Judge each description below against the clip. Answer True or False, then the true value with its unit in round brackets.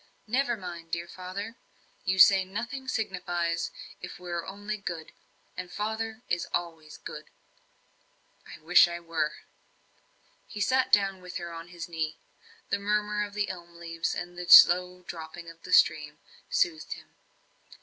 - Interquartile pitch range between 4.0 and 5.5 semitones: False (3.5 semitones)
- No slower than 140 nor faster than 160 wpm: True (150 wpm)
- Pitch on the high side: False (180 Hz)